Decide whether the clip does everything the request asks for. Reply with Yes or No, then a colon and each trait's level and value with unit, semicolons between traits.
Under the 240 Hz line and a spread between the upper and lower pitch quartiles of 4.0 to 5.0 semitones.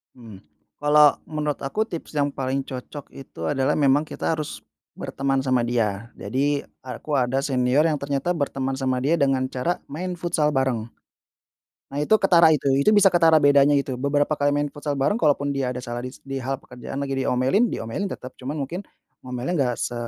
No: medium, 140 Hz; narrow, 2.5 semitones